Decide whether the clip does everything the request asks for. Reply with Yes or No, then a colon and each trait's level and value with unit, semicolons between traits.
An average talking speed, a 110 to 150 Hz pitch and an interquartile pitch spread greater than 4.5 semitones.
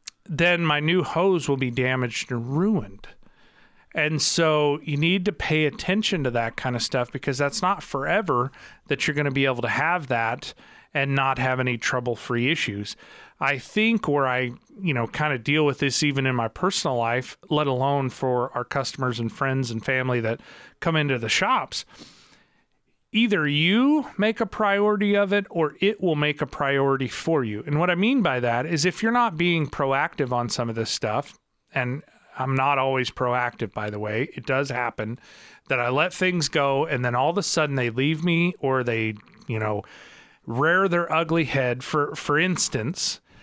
Yes: average, 190 wpm; medium, 140 Hz; average, 5.2 semitones